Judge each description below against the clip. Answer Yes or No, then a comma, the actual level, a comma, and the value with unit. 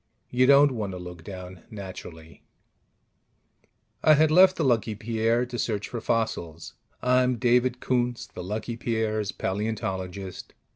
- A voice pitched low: Yes, low, 110 Hz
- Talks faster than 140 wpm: No, slow, 135 wpm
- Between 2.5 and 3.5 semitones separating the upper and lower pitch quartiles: No, average, 4.5 semitones